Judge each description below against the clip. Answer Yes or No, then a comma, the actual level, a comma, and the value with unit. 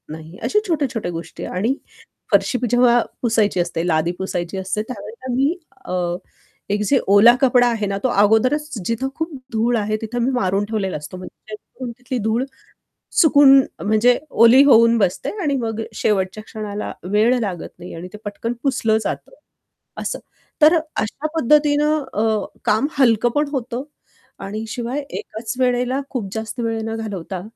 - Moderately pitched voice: No, high, 225 Hz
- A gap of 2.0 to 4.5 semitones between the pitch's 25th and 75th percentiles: Yes, average, 4.0 semitones